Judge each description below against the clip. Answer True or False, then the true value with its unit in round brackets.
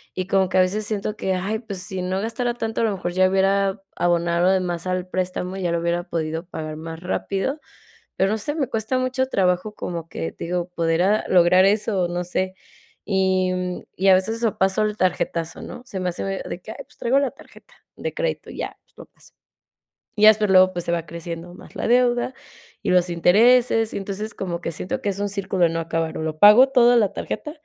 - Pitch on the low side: False (190 Hz)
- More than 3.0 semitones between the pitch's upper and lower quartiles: True (3.5 semitones)